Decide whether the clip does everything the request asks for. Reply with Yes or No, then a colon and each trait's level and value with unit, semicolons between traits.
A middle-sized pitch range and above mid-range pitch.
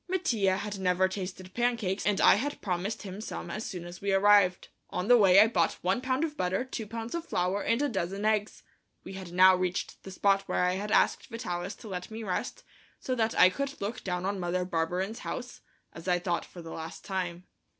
Yes: average, 3.5 semitones; high, 195 Hz